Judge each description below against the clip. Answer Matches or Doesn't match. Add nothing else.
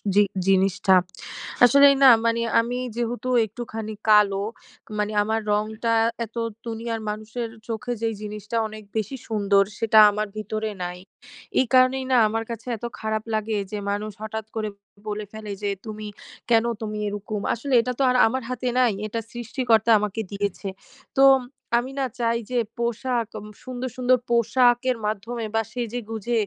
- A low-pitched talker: Doesn't match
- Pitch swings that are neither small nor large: Doesn't match